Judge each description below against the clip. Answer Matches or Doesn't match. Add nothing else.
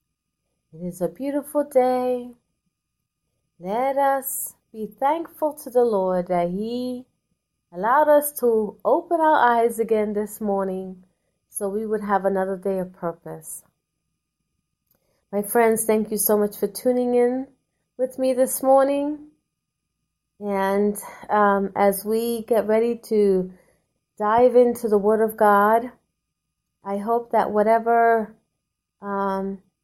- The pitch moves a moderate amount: Matches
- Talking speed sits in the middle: Doesn't match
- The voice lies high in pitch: Matches